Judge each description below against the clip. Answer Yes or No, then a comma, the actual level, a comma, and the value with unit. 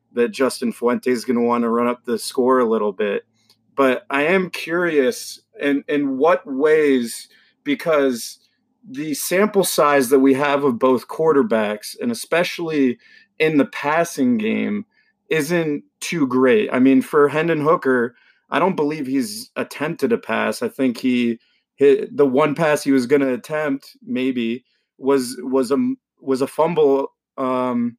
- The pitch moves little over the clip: No, wide, 5.5 semitones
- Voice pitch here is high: No, medium, 140 Hz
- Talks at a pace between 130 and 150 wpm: No, average, 160 wpm